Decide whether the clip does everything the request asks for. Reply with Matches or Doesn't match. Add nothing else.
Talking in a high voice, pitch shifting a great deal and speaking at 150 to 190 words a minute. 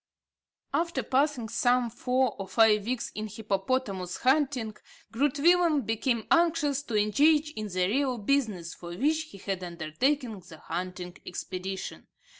Doesn't match